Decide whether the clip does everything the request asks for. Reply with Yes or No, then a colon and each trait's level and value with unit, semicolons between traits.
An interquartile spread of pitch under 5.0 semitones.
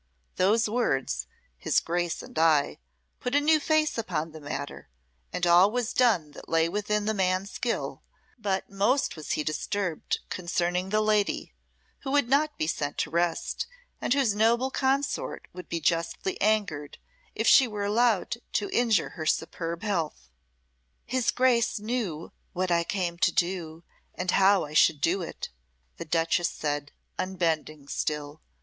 No: average, 5.3 semitones